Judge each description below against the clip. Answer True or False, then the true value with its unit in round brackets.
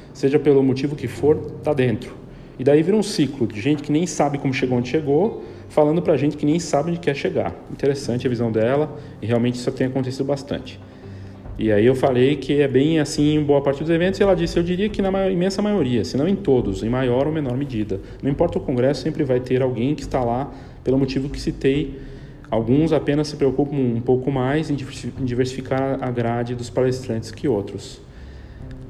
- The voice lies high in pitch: False (135 Hz)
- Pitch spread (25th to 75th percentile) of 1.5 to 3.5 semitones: True (2.9 semitones)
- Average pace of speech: False (210 wpm)